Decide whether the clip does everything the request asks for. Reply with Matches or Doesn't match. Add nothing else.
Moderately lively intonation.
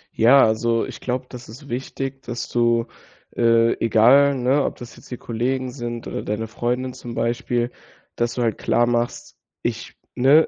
Doesn't match